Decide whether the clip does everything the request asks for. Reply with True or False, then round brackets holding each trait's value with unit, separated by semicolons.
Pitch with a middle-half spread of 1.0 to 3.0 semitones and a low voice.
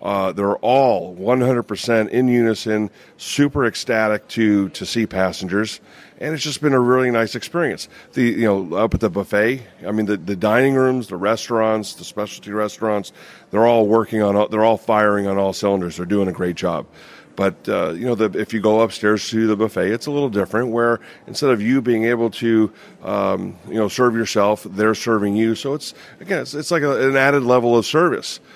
True (2.7 semitones; 110 Hz)